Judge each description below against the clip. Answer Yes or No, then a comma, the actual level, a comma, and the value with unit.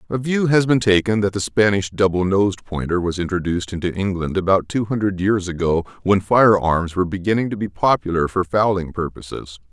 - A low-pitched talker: Yes, very low, 95 Hz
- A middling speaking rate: Yes, average, 190 wpm